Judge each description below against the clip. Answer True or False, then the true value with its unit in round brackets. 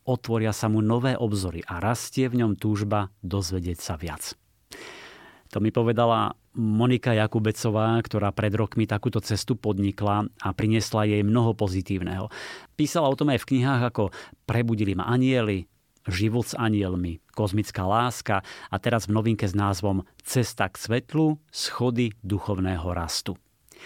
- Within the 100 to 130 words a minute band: False (140 wpm)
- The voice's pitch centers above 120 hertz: False (110 Hz)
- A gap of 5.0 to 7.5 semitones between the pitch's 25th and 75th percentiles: False (2.9 semitones)